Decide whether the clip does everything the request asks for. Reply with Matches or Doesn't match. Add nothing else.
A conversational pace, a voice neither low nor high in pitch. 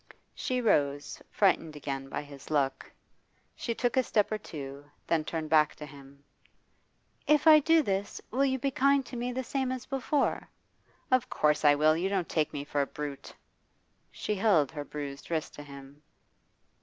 Matches